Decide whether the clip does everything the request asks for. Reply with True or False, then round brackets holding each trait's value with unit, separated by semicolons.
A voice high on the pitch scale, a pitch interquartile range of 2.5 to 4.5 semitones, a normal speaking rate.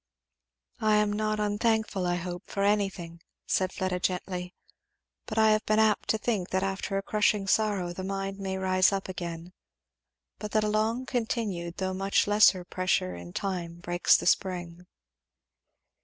True (195 Hz; 2.8 semitones; 160 wpm)